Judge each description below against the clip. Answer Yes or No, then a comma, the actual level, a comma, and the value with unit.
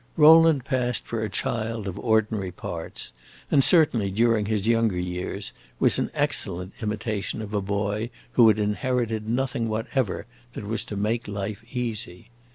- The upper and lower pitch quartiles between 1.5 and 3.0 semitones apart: Yes, narrow, 2.5 semitones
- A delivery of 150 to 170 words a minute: Yes, average, 155 wpm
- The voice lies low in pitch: Yes, low, 110 Hz